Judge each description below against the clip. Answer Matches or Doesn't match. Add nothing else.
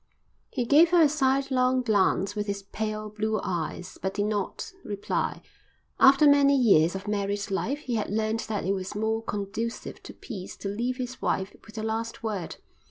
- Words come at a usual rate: Matches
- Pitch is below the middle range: Doesn't match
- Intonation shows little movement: Doesn't match